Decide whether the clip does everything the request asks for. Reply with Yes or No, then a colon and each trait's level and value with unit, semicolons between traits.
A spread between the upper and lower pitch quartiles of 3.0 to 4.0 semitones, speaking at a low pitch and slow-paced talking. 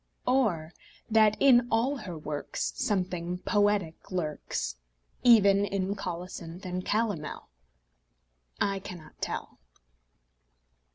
No: average, 3.6 semitones; high, 195 Hz; slow, 95 wpm